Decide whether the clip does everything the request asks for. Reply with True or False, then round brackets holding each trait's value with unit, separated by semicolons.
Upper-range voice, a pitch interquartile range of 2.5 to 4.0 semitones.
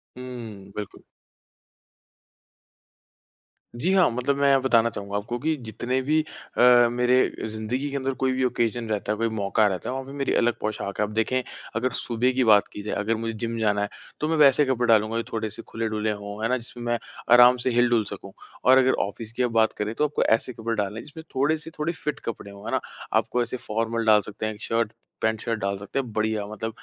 False (115 Hz; 2.9 semitones)